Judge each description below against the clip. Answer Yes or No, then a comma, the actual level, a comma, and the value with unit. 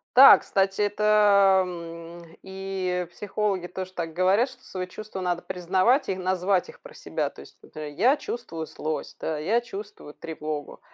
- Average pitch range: Yes, average, 3.3 semitones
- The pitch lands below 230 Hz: Yes, medium, 185 Hz